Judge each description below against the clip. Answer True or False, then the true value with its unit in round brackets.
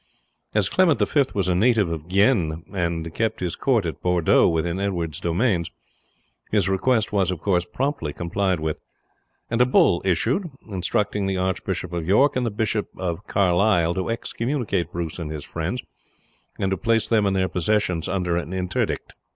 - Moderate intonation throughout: True (3.9 semitones)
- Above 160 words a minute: True (170 wpm)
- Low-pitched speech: True (95 Hz)